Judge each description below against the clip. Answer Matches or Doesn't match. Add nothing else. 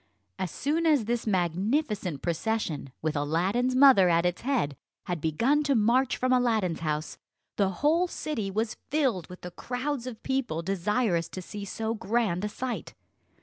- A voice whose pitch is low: Doesn't match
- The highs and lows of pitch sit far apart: Matches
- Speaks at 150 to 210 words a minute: Matches